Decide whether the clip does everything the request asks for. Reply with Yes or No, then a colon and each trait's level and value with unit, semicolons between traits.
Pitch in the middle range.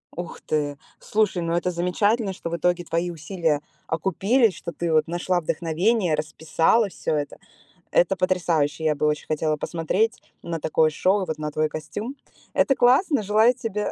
Yes: medium, 175 Hz